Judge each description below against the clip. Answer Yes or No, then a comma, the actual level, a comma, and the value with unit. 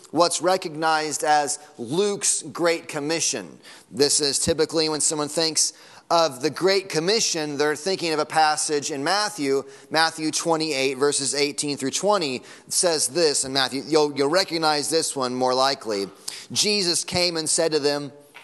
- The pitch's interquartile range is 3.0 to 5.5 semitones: No, narrow, 2.5 semitones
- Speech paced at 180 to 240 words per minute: No, average, 150 wpm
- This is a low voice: No, medium, 155 Hz